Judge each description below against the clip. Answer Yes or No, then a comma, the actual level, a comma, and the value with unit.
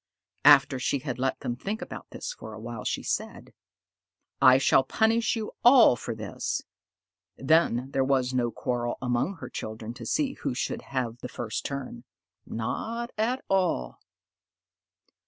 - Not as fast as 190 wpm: Yes, average, 155 wpm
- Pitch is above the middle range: No, low, 135 Hz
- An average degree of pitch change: No, wide, 8.6 semitones